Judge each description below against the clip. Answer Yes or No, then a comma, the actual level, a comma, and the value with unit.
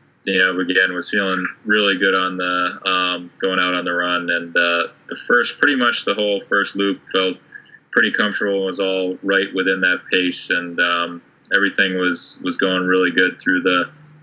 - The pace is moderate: Yes, average, 190 wpm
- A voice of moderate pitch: No, very low, 95 Hz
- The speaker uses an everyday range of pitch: No, narrow, 1.3 semitones